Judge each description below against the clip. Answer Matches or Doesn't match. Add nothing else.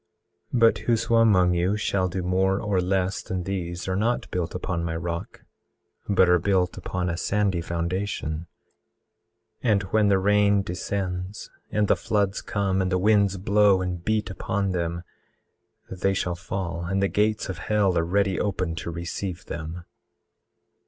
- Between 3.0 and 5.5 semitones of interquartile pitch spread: Doesn't match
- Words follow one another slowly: Doesn't match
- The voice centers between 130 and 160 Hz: Doesn't match